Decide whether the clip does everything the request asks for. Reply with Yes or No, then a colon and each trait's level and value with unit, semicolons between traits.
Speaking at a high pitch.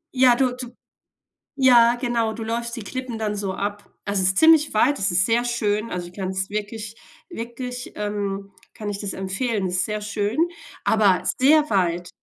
Yes: high, 215 Hz